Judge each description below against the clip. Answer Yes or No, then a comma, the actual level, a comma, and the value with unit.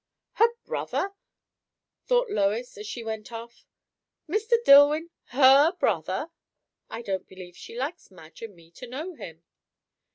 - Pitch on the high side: Yes, high, 245 Hz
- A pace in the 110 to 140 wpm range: Yes, slow, 135 wpm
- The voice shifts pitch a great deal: Yes, wide, 8.0 semitones